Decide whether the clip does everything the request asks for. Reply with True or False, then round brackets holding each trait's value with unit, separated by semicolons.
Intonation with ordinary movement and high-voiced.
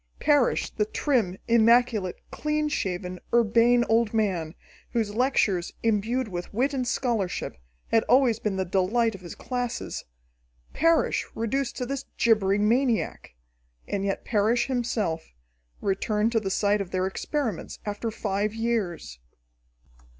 True (3.8 semitones; 220 Hz)